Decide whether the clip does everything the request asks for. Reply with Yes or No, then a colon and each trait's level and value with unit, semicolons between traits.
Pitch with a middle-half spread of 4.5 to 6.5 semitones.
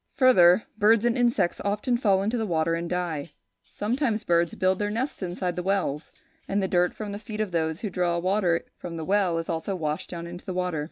No: average, 3.7 semitones